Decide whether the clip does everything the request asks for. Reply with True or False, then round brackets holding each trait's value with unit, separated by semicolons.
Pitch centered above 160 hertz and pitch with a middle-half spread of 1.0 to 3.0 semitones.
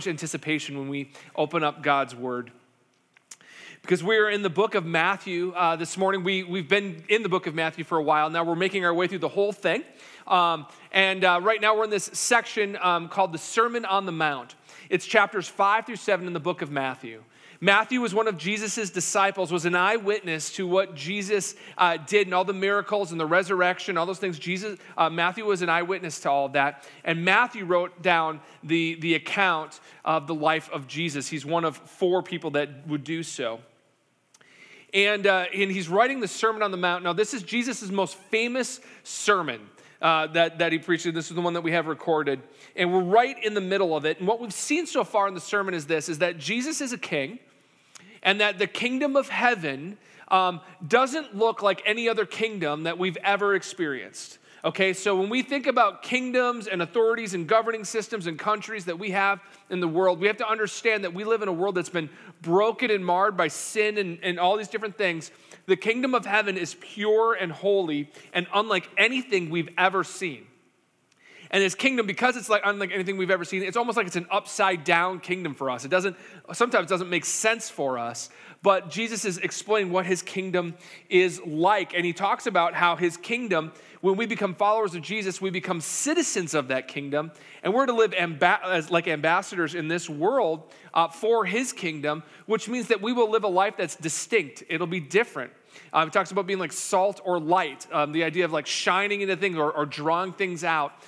False (185 Hz; 3.8 semitones)